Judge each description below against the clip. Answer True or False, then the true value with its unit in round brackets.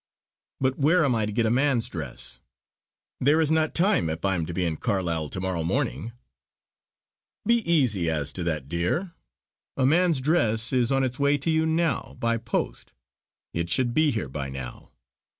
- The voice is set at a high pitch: False (115 Hz)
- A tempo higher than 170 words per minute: True (185 wpm)